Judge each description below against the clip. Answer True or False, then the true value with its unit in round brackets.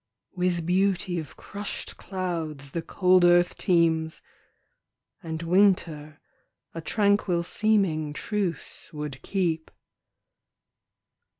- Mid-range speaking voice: True (175 Hz)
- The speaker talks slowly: True (90 wpm)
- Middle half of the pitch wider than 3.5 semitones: False (2.9 semitones)